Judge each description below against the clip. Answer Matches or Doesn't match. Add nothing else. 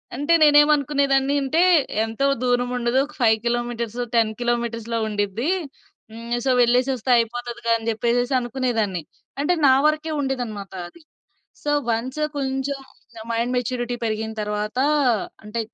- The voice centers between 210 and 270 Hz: Matches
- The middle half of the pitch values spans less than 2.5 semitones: Doesn't match